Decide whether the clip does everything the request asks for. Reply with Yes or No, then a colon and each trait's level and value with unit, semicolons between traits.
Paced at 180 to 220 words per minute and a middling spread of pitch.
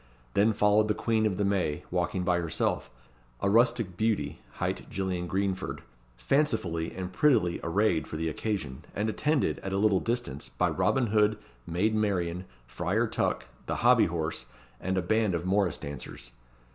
No: average, 160 wpm; average, 4.1 semitones